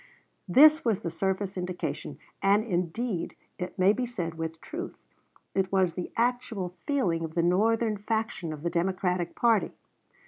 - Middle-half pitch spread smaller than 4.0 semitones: No, average, 4.6 semitones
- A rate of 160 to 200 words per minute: No, average, 150 wpm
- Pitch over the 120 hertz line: Yes, high, 190 Hz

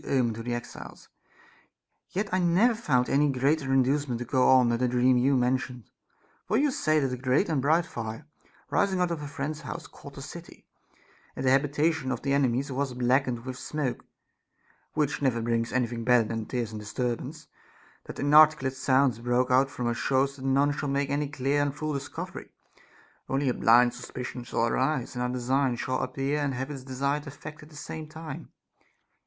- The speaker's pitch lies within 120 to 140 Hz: Yes, low, 135 Hz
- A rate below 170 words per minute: No, average, 195 wpm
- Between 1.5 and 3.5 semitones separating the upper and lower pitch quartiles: Yes, average, 2.9 semitones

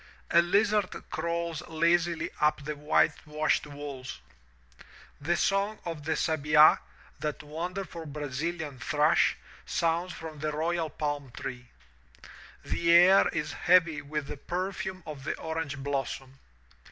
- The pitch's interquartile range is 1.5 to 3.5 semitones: Yes, average, 2.7 semitones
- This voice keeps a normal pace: No, slow, 120 wpm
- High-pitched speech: No, medium, 155 Hz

